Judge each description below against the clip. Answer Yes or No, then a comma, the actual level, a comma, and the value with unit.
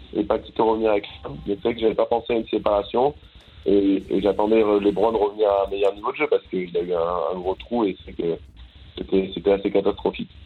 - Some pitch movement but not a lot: No, narrow, 2.3 semitones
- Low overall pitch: Yes, low, 100 Hz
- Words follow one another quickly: Yes, fast, 260 wpm